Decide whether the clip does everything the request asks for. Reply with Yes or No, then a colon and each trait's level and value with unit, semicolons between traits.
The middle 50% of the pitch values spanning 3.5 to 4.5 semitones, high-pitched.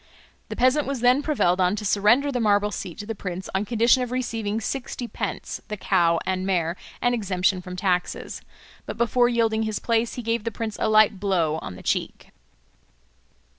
Yes: average, 4.2 semitones; high, 215 Hz